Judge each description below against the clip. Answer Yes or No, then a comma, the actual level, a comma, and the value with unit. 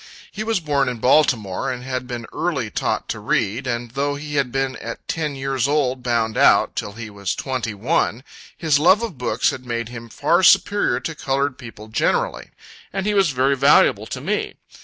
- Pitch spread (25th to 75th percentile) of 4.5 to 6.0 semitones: No, average, 4.0 semitones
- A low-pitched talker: Yes, low, 130 Hz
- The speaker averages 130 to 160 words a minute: No, average, 195 wpm